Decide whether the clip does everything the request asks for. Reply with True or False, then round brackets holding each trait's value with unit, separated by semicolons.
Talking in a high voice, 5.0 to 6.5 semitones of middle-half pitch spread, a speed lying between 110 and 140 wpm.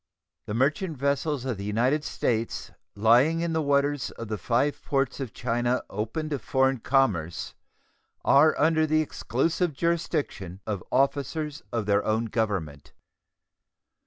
False (135 Hz; 5.3 semitones; 135 wpm)